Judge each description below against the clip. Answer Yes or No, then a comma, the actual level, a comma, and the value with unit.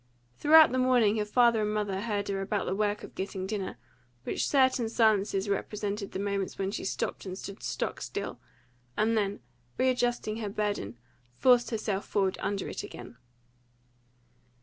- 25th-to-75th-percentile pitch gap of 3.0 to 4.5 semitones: No, narrow, 2.5 semitones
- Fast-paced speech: No, average, 165 wpm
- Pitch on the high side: Yes, high, 210 Hz